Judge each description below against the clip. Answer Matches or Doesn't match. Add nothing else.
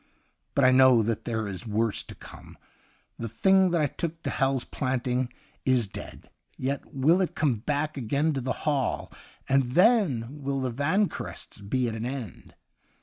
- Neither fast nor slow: Matches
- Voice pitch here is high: Doesn't match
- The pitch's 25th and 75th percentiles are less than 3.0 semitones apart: Doesn't match